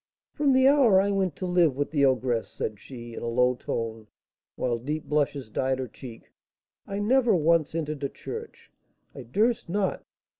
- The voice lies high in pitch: No, medium, 150 Hz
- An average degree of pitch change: No, wide, 7.8 semitones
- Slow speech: No, average, 180 wpm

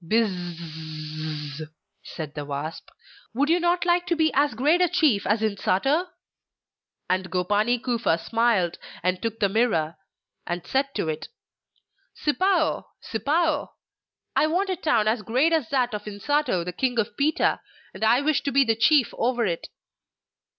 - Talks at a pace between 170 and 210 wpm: No, average, 155 wpm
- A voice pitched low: No, high, 230 Hz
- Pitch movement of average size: No, wide, 8.6 semitones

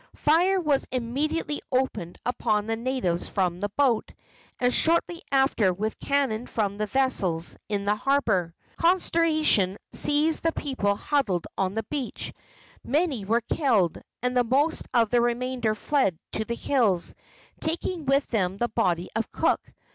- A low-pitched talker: No, high, 240 Hz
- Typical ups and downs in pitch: No, wide, 5.7 semitones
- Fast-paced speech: No, average, 145 wpm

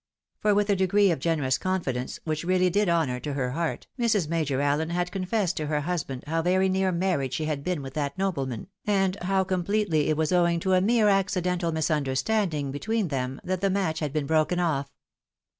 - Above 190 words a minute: Yes, fast, 205 wpm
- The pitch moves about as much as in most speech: Yes, average, 4.3 semitones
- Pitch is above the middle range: No, medium, 170 Hz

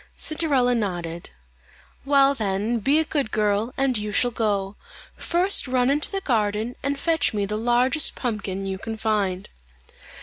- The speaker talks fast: No, average, 155 wpm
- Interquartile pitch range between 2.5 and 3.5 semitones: No, average, 5.1 semitones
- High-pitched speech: Yes, high, 230 Hz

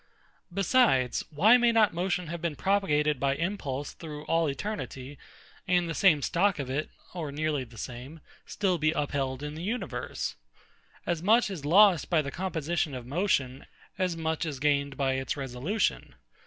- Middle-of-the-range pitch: Yes, medium, 155 Hz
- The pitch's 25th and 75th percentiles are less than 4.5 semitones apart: No, average, 4.8 semitones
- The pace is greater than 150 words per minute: Yes, average, 165 wpm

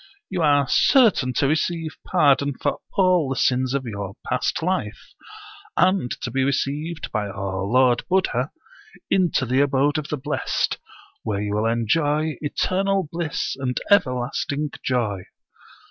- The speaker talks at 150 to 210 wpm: No, average, 140 wpm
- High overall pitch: No, medium, 140 Hz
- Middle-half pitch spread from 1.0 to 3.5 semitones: No, average, 4.7 semitones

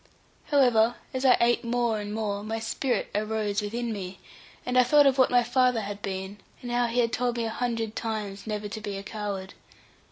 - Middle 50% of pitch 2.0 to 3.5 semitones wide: Yes, average, 2.8 semitones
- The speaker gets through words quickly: Yes, fast, 210 wpm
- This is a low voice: No, high, 225 Hz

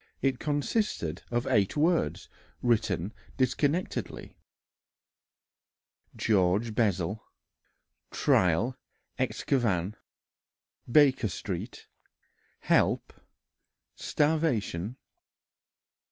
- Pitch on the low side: Yes, low, 115 Hz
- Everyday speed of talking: No, slow, 55 wpm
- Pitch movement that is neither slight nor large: No, wide, 6.9 semitones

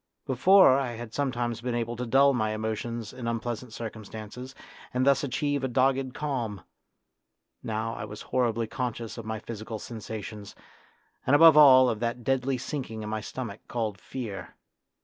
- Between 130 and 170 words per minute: No, average, 180 wpm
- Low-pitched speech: Yes, low, 120 Hz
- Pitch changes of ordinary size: Yes, average, 3.0 semitones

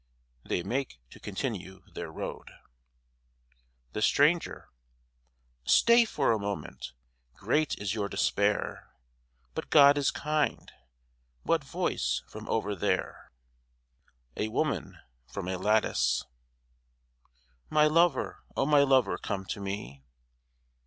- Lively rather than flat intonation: Yes, wide, 6.8 semitones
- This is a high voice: No, low, 110 Hz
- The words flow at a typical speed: No, slow, 110 wpm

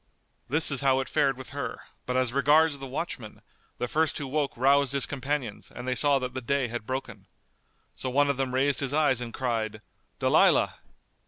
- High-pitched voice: No, low, 135 Hz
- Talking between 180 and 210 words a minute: Yes, average, 195 wpm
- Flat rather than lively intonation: Yes, narrow, 2.1 semitones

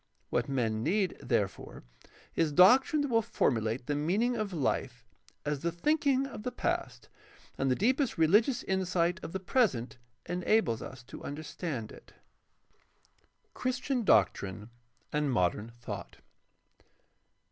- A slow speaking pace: Yes, slow, 125 wpm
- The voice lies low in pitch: No, medium, 170 Hz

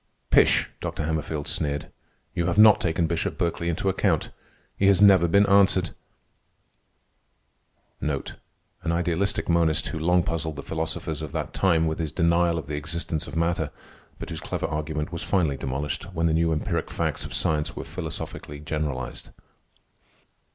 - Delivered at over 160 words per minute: No, average, 155 wpm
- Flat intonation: Yes, narrow, 2.1 semitones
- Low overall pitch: Yes, very low, 80 Hz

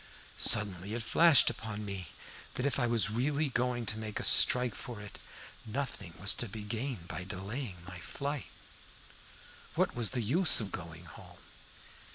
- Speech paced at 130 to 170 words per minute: Yes, average, 165 wpm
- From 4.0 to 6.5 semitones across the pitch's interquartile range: Yes, average, 4.3 semitones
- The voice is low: Yes, low, 110 Hz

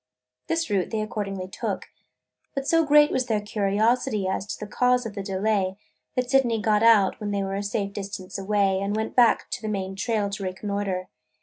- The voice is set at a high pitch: Yes, high, 205 Hz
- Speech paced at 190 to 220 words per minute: Yes, average, 200 wpm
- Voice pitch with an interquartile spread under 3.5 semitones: Yes, average, 2.7 semitones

